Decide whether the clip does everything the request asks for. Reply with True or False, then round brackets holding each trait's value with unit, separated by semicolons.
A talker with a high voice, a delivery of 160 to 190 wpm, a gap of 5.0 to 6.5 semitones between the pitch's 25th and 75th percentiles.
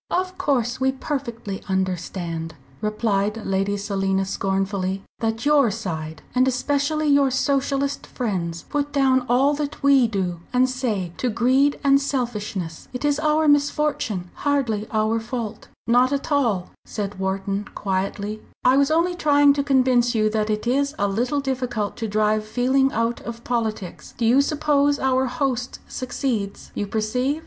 False (240 Hz; 150 wpm; 5.3 semitones)